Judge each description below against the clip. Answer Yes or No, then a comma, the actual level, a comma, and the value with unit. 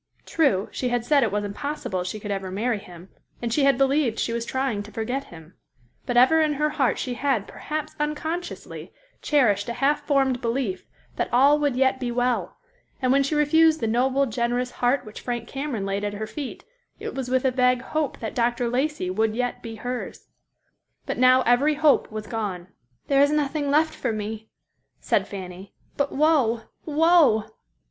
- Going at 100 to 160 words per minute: No, average, 185 wpm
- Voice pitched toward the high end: Yes, very high, 250 Hz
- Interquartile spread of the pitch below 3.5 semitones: No, average, 4.5 semitones